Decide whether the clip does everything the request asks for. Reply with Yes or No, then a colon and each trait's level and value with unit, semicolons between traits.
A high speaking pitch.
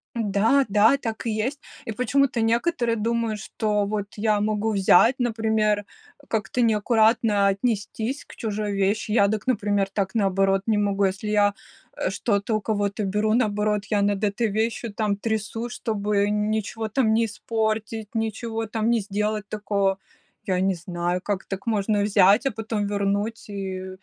Yes: high, 210 Hz